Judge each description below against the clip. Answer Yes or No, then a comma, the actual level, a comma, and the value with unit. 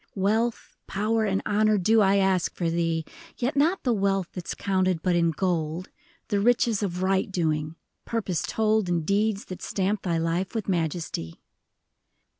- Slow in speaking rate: No, average, 170 wpm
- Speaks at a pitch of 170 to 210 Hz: Yes, high, 190 Hz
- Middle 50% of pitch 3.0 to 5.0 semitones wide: Yes, average, 3.8 semitones